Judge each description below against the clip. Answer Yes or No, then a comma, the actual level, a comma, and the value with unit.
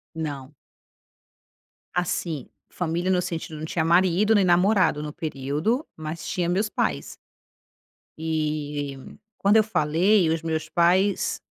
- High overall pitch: No, medium, 165 Hz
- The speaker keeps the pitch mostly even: No, average, 3.4 semitones